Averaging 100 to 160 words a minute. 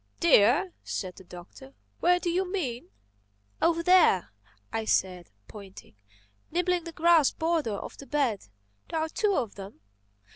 Yes: average, 140 wpm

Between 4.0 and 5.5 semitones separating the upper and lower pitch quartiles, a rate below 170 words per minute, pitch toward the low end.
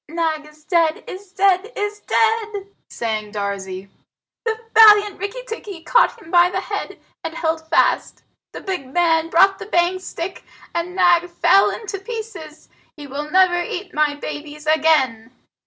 No: average, 4.6 semitones; average, 155 wpm; very high, 345 Hz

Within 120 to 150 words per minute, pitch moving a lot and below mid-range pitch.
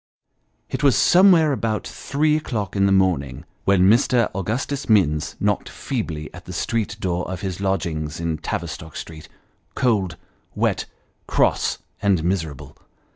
Yes: slow, 135 wpm; wide, 6.1 semitones; very low, 95 Hz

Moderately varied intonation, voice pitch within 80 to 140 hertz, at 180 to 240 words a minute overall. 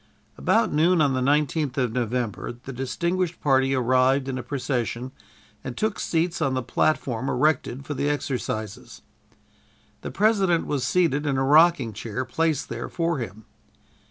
No: average, 4.1 semitones; low, 135 Hz; average, 155 wpm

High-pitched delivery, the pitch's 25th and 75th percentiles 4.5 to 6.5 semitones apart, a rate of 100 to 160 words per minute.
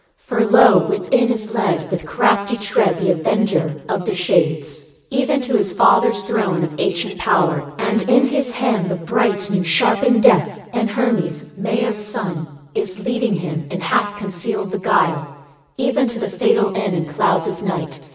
No: high, 200 Hz; wide, 5.4 semitones; average, 170 wpm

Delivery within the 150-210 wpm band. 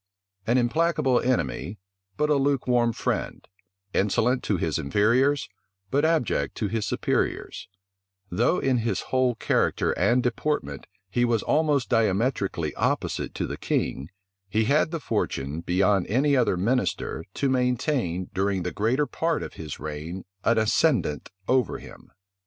No: average, 140 wpm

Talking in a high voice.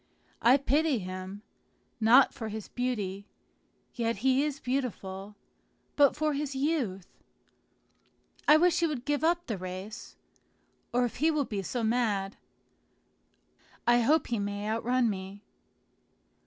Yes: high, 240 Hz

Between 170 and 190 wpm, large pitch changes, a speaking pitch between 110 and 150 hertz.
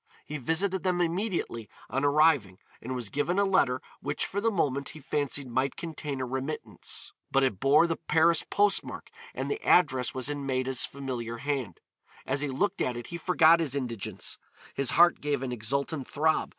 No: average, 180 wpm; average, 4.2 semitones; medium, 140 Hz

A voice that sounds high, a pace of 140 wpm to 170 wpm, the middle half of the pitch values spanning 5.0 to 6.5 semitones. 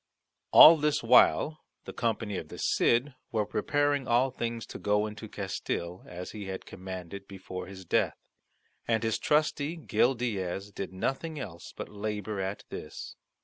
No: low, 105 Hz; average, 155 wpm; average, 5.3 semitones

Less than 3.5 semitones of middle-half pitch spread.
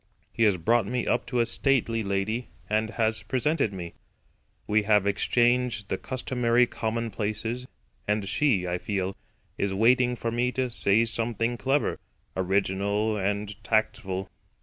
Yes: average, 3.1 semitones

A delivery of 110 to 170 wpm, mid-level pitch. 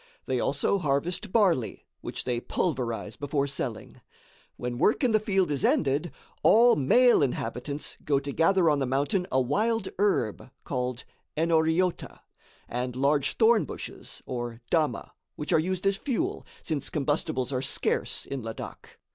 Yes: average, 145 wpm; medium, 150 Hz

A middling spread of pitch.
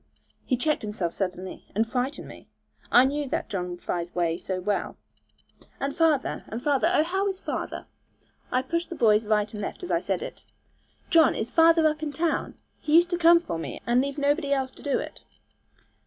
No: wide, 7.4 semitones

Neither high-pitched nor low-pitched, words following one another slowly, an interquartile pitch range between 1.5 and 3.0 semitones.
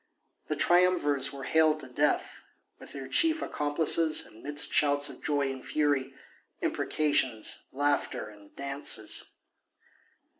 Yes: medium, 145 Hz; slow, 115 wpm; narrow, 2.4 semitones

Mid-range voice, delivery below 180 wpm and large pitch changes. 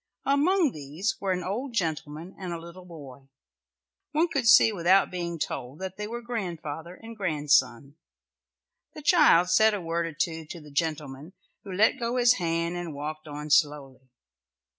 Yes: medium, 170 Hz; average, 165 wpm; wide, 5.8 semitones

